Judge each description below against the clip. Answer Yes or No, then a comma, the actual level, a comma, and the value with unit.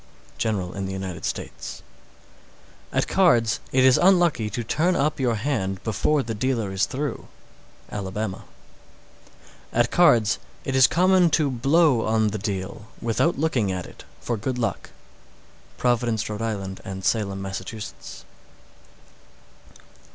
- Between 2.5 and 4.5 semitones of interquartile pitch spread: No, average, 5.0 semitones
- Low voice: Yes, low, 115 Hz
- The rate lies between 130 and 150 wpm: Yes, slow, 135 wpm